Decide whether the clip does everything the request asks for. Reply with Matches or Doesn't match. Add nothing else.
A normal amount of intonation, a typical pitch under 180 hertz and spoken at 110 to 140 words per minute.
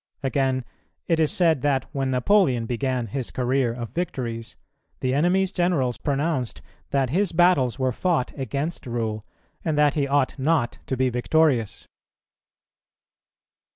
Matches